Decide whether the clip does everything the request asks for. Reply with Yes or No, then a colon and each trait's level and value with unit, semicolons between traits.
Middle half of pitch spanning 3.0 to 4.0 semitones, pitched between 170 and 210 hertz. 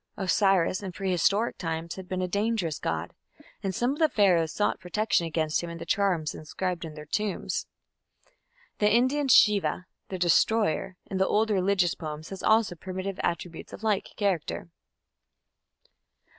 Yes: average, 3.6 semitones; high, 190 Hz